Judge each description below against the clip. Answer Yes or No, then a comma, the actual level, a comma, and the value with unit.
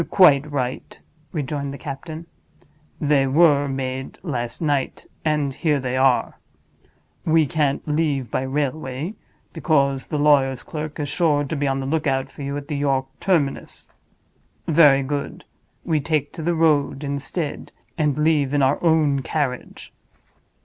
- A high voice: No, medium, 145 Hz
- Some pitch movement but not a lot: No, narrow, 2.3 semitones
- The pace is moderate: Yes, average, 145 wpm